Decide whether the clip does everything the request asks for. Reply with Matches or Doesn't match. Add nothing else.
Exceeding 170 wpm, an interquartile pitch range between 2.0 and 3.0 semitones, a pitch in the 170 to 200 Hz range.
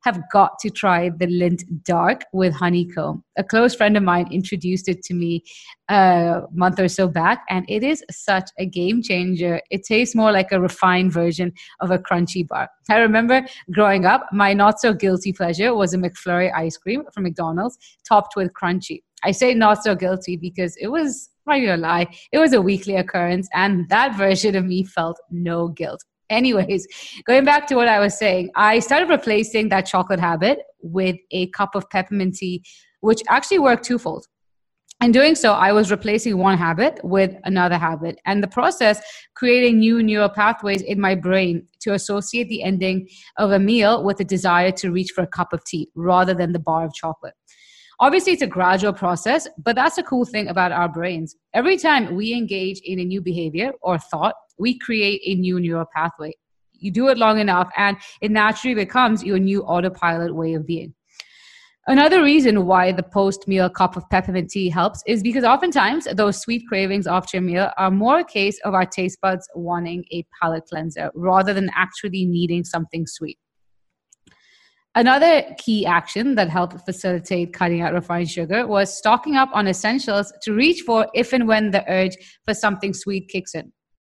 Doesn't match